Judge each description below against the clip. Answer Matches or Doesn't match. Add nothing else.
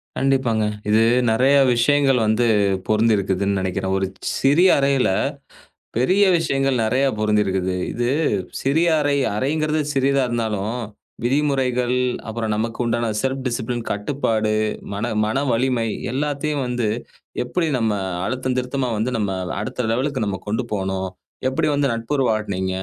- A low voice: Matches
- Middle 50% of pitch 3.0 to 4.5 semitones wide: Matches